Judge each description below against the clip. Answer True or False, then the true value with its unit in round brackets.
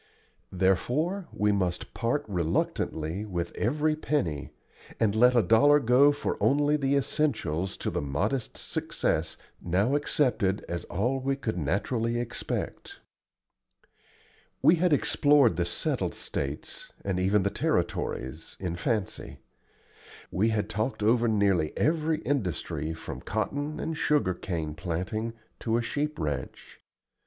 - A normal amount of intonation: False (7.9 semitones)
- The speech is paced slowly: True (125 wpm)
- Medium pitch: False (110 Hz)